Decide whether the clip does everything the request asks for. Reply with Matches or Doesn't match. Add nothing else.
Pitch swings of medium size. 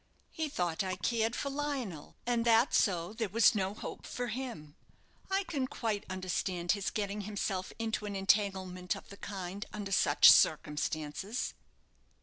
Matches